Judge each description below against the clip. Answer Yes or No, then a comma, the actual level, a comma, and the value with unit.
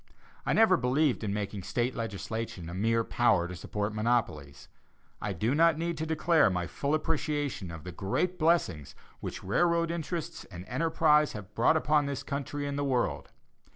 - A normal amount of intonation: No, wide, 7.7 semitones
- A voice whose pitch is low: Yes, low, 125 Hz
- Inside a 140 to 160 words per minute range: No, average, 170 wpm